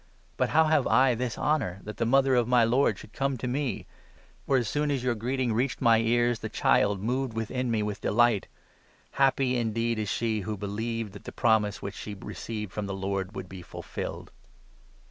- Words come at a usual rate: No, fast, 210 wpm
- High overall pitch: No, low, 115 Hz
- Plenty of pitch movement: No, average, 3.3 semitones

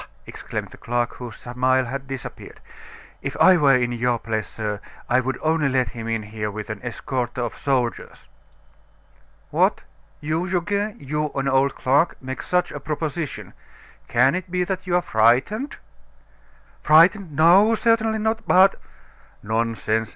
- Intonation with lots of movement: Yes, wide, 6.6 semitones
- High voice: No, low, 135 Hz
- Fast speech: No, average, 150 wpm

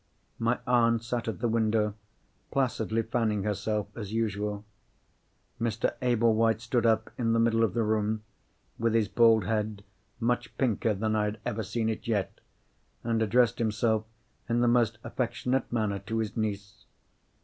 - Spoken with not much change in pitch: Yes, narrow, 1.6 semitones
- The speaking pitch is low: Yes, low, 110 Hz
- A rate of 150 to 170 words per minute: Yes, average, 155 wpm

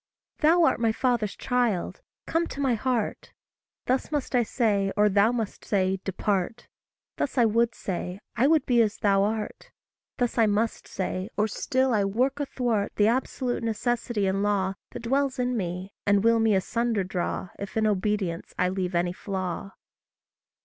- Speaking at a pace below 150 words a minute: No, average, 170 wpm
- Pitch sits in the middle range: No, high, 220 Hz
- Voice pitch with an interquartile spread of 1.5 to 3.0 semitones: No, average, 3.8 semitones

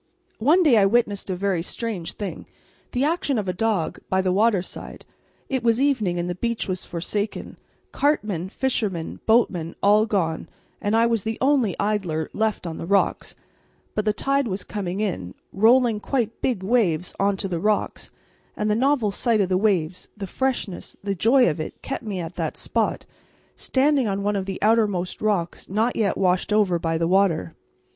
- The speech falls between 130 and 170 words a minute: No, average, 180 wpm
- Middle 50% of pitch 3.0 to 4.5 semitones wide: Yes, average, 3.9 semitones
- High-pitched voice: Yes, high, 205 Hz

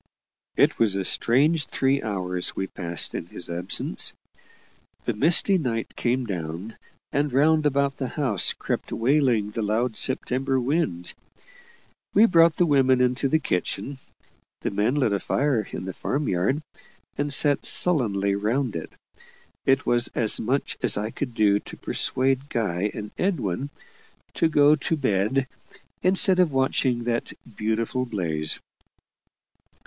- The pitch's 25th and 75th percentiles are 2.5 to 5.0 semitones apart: No, wide, 5.5 semitones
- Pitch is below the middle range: Yes, low, 125 Hz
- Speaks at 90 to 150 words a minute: Yes, average, 145 wpm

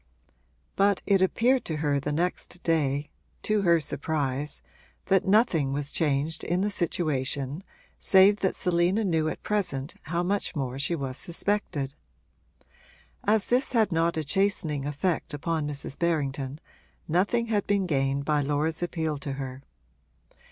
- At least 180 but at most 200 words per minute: No, average, 145 wpm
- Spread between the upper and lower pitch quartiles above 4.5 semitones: Yes, average, 5.0 semitones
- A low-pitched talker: No, medium, 160 Hz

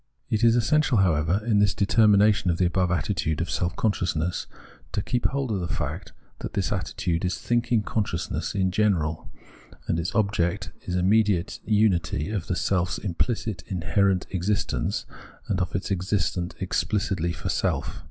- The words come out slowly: No, average, 160 wpm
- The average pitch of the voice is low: Yes, very low, 95 Hz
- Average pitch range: Yes, average, 3.4 semitones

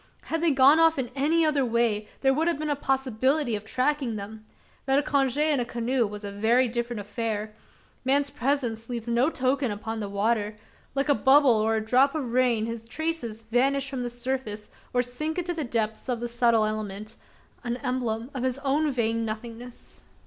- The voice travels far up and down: No, average, 3.7 semitones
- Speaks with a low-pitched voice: No, high, 245 Hz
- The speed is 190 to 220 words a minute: Yes, average, 195 wpm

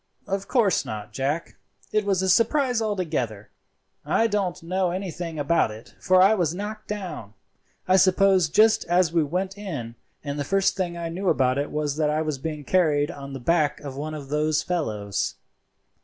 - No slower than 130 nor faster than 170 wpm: No, average, 185 wpm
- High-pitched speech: No, medium, 170 Hz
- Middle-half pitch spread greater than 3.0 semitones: Yes, average, 4.8 semitones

